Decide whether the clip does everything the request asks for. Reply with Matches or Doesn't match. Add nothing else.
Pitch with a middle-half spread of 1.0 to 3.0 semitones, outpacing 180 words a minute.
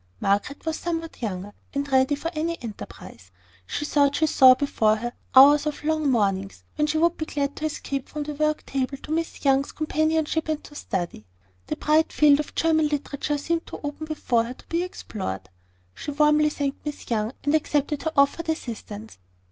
Doesn't match